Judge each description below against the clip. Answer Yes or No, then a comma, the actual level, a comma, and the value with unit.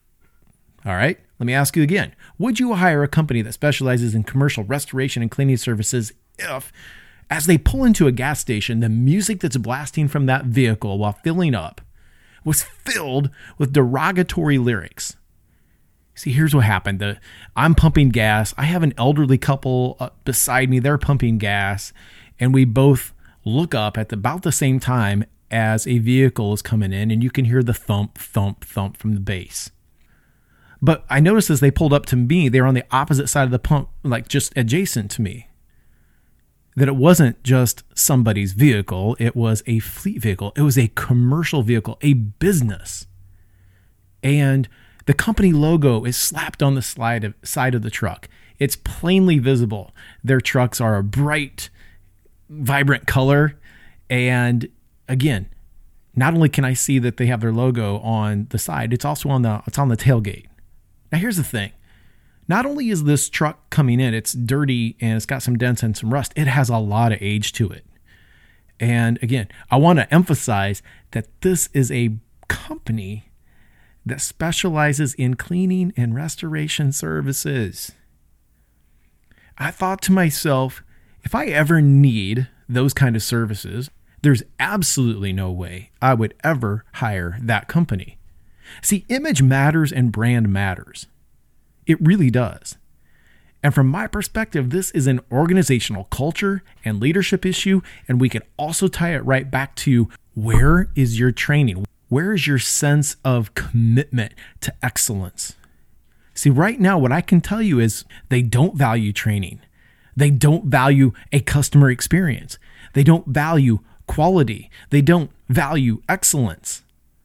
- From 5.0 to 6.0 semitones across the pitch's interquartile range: Yes, average, 5.3 semitones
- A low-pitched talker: Yes, low, 125 Hz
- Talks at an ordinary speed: Yes, average, 160 wpm